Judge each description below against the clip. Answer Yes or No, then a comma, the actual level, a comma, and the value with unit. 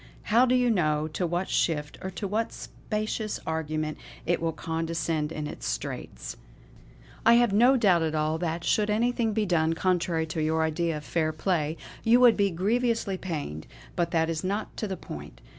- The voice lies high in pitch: No, medium, 170 Hz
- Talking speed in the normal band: Yes, average, 175 wpm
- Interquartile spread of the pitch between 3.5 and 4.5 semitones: No, average, 5.0 semitones